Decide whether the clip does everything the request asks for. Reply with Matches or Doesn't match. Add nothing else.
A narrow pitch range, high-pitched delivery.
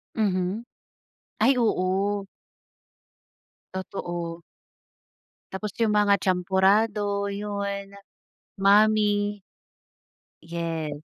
Matches